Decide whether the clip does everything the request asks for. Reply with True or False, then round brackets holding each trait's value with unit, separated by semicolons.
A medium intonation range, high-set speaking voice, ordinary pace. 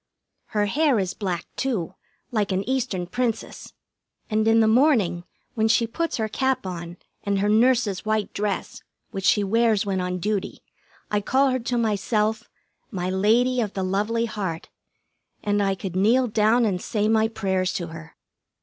True (3.3 semitones; 210 Hz; 170 wpm)